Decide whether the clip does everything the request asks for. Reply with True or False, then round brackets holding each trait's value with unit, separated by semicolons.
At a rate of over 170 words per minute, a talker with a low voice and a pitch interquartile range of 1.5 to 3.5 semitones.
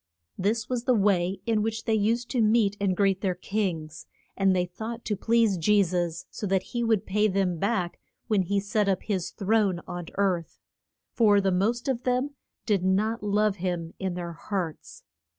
False (190 wpm; 200 Hz; 3.2 semitones)